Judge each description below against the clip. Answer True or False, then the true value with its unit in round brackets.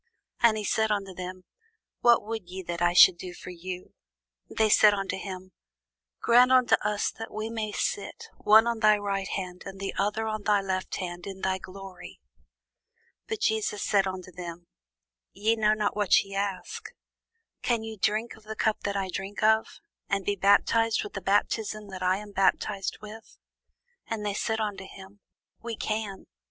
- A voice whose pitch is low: False (205 Hz)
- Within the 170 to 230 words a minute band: True (180 wpm)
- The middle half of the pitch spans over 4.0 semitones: False (2.4 semitones)